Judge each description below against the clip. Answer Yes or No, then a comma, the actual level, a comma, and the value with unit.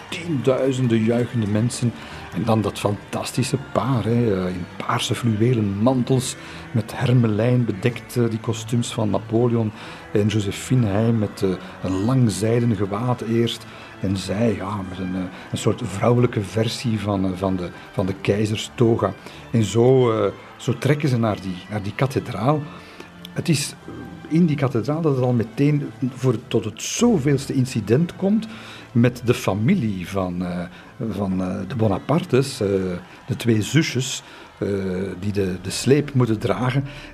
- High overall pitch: No, low, 115 Hz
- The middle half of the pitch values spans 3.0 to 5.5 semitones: Yes, average, 3.9 semitones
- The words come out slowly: No, average, 145 wpm